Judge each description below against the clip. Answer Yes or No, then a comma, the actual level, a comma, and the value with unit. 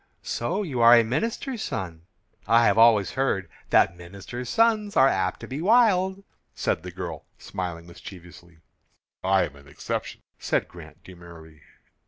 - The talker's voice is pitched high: No, low, 110 Hz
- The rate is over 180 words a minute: No, average, 150 wpm